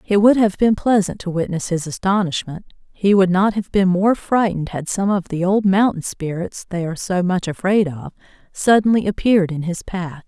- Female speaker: Yes, female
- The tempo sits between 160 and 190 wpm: No, average, 200 wpm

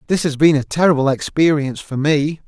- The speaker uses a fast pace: No, average, 195 wpm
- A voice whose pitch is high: No, medium, 150 Hz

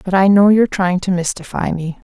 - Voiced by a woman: Yes, female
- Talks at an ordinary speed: No, fast, 230 wpm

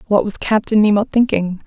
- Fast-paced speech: No, average, 180 wpm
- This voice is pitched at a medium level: No, high, 210 Hz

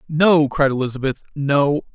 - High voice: No, medium, 145 Hz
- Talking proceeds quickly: No, slow, 95 wpm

